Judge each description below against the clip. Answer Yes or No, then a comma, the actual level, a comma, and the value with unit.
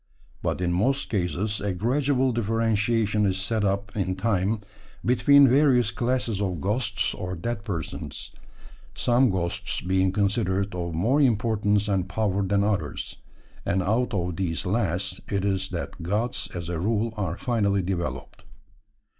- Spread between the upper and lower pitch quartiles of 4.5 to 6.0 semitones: No, average, 3.6 semitones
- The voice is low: Yes, low, 100 Hz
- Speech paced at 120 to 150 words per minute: Yes, average, 145 wpm